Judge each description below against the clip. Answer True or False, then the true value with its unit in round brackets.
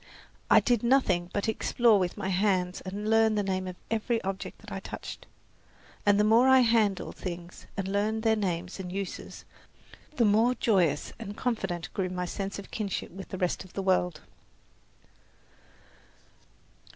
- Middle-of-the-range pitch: False (200 Hz)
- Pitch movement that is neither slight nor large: True (3.3 semitones)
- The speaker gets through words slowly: False (165 wpm)